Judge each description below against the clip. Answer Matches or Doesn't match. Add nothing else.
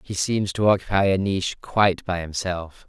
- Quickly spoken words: Doesn't match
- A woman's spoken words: Doesn't match